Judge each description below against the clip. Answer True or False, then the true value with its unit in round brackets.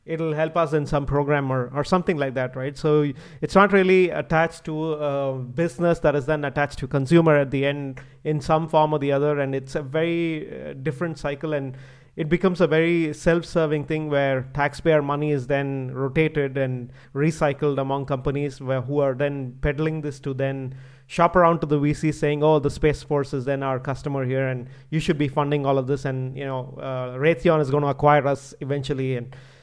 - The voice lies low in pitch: False (145 Hz)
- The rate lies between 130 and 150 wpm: False (205 wpm)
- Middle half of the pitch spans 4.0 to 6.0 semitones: False (2.5 semitones)